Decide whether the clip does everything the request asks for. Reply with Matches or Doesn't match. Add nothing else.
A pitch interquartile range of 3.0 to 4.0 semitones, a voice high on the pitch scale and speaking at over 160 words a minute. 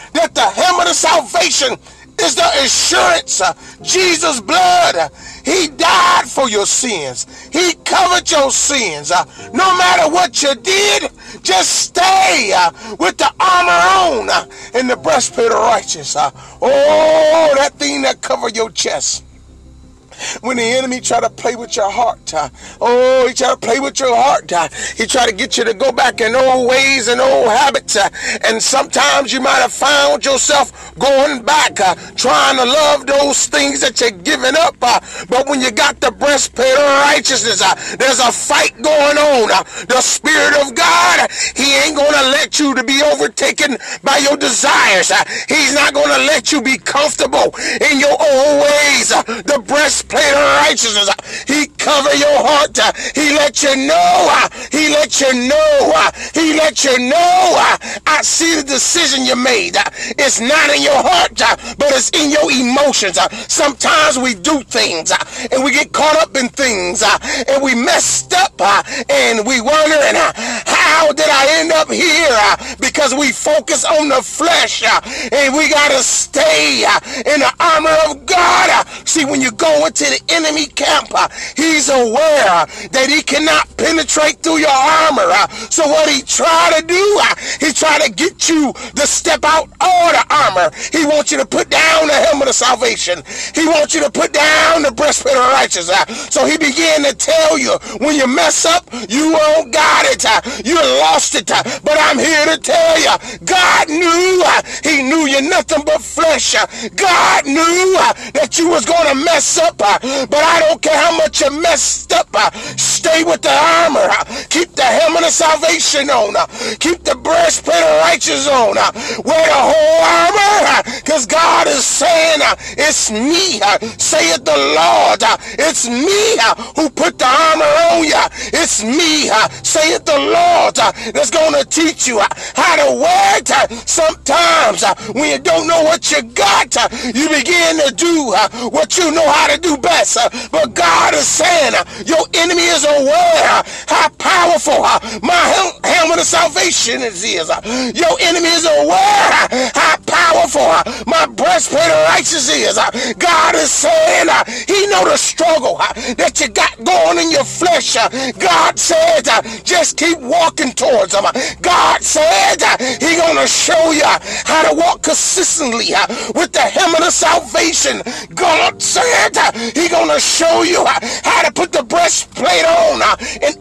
Matches